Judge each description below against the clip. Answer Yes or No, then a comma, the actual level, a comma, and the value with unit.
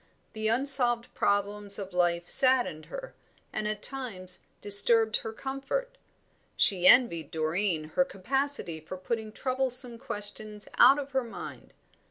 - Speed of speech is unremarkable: No, slow, 130 wpm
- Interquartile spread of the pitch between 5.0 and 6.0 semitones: Yes, wide, 5.4 semitones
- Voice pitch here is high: Yes, high, 220 Hz